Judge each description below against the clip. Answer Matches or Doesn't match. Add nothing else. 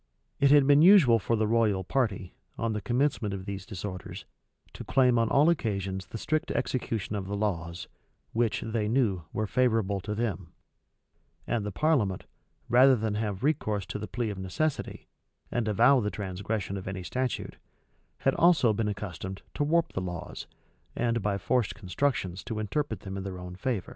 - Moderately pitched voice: Doesn't match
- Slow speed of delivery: Doesn't match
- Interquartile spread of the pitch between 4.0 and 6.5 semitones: Matches